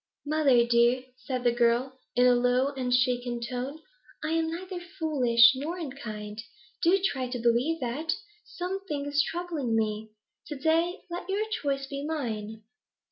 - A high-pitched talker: Yes, very high, 265 Hz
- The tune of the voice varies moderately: Yes, average, 4.9 semitones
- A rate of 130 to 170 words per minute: Yes, average, 150 wpm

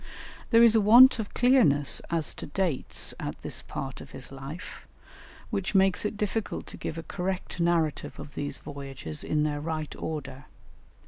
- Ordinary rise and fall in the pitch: No, wide, 6.0 semitones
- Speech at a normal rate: Yes, average, 170 wpm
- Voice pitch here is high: No, medium, 160 Hz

